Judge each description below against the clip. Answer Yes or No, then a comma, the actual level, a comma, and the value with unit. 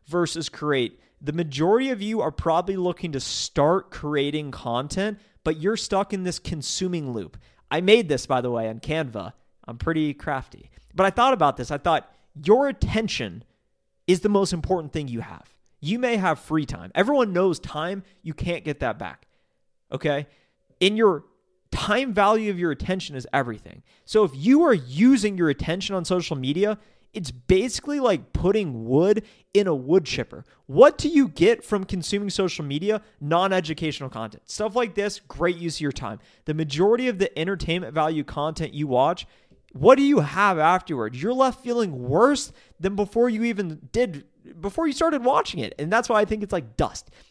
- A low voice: No, medium, 175 Hz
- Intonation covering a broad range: Yes, wide, 6.2 semitones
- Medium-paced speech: Yes, average, 185 wpm